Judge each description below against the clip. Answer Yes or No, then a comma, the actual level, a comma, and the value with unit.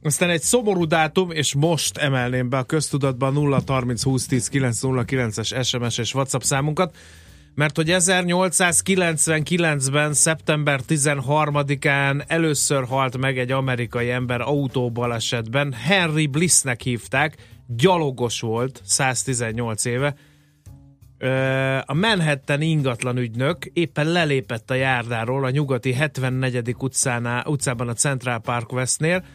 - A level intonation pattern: No, average, 3.4 semitones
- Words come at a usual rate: No, slow, 100 wpm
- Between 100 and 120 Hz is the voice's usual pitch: No, low, 135 Hz